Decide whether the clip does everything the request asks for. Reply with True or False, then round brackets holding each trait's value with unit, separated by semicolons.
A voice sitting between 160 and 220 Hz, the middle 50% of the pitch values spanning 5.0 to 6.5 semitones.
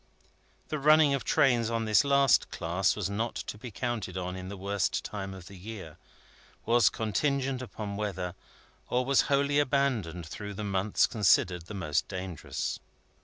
False (105 Hz; 5.3 semitones)